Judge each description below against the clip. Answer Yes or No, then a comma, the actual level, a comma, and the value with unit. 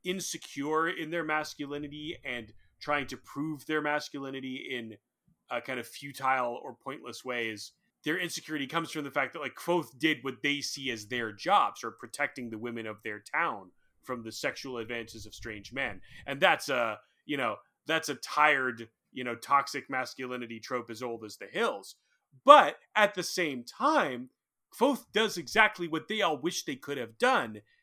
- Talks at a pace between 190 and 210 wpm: No, average, 175 wpm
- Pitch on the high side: No, medium, 140 Hz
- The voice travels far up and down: No, average, 4.7 semitones